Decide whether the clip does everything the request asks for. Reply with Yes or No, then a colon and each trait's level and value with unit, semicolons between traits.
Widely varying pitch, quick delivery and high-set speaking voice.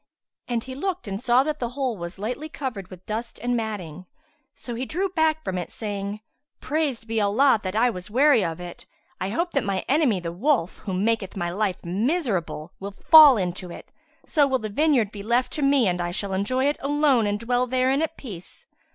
Yes: wide, 6.1 semitones; fast, 210 wpm; high, 230 Hz